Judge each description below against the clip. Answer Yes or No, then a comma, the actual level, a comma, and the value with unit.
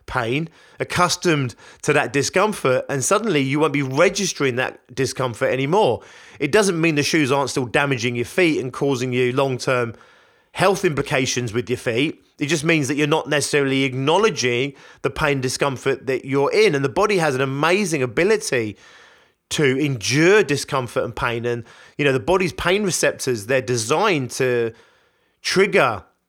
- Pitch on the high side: No, medium, 140 Hz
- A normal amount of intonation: Yes, average, 4.5 semitones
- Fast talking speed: No, average, 165 wpm